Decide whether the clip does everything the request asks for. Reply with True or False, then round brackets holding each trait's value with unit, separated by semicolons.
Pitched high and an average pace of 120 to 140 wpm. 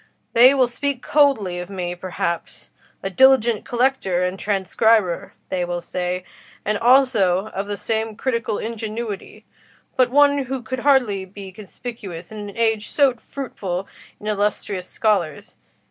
True (215 Hz; 135 wpm)